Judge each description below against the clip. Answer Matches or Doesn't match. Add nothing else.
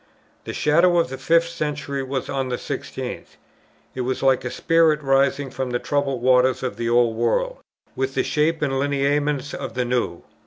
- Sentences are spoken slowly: Doesn't match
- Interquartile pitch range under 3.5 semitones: Matches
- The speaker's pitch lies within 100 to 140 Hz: Matches